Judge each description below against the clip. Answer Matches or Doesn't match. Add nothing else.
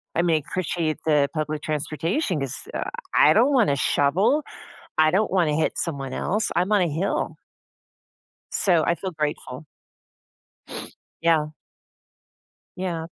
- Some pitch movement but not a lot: Matches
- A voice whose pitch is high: Doesn't match